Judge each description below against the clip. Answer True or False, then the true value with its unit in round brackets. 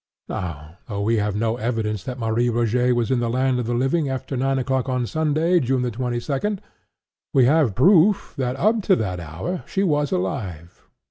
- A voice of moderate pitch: False (125 Hz)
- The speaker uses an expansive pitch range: False (4.4 semitones)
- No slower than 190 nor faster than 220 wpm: True (195 wpm)